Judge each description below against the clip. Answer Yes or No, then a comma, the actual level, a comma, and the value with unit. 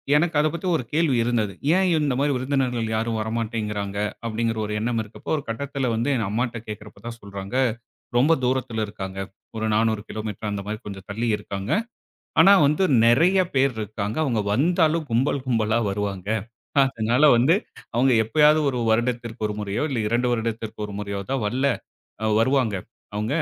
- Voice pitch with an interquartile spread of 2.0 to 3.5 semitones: No, average, 3.9 semitones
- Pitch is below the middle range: Yes, low, 115 Hz